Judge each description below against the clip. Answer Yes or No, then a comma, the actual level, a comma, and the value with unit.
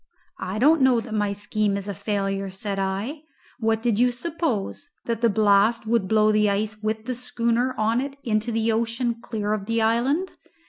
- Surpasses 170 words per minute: Yes, average, 190 wpm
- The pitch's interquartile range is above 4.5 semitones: No, narrow, 2.5 semitones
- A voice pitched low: No, high, 220 Hz